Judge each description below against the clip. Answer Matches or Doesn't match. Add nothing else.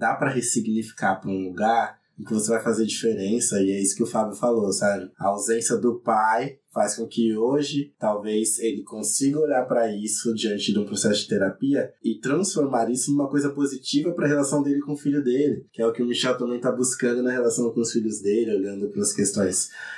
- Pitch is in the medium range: Doesn't match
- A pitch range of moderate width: Matches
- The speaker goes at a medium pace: Doesn't match